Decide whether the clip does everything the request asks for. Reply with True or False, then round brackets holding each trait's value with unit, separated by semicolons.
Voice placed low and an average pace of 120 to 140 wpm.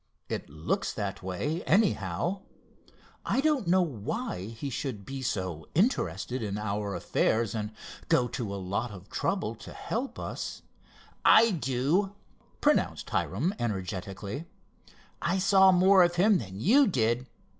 True (125 Hz; 135 wpm)